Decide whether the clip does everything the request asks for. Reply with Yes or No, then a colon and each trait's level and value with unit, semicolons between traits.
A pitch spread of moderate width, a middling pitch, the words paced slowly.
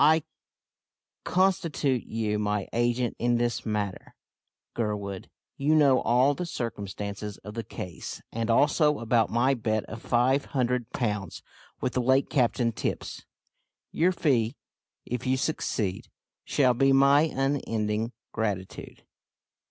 No: average, 4.0 semitones; low, 120 Hz; slow, 125 wpm